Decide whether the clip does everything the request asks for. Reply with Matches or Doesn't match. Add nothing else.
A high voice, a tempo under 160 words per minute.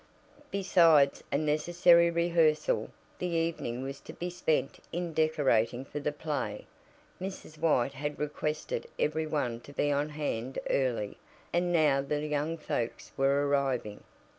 Doesn't match